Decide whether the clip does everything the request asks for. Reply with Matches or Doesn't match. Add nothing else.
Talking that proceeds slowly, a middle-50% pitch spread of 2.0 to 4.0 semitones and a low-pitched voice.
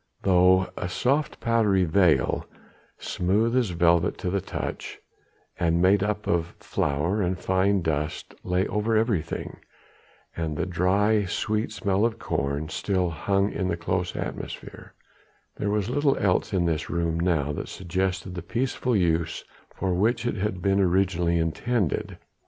Doesn't match